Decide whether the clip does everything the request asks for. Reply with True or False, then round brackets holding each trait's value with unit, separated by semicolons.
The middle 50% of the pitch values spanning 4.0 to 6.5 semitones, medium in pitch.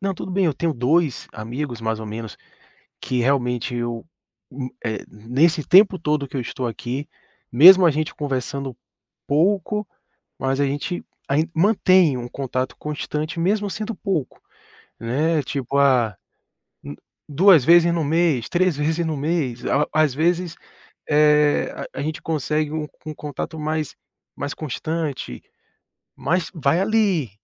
True (4.5 semitones; 150 Hz)